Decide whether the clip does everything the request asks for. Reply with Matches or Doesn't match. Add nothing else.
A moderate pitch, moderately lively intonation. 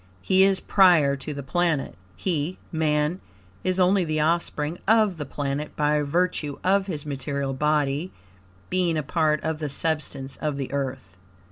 Matches